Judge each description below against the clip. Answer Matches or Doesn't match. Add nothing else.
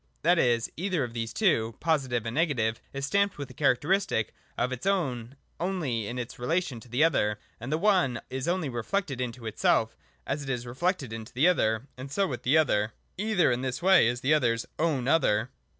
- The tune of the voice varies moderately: Doesn't match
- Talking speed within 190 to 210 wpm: Matches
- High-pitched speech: Doesn't match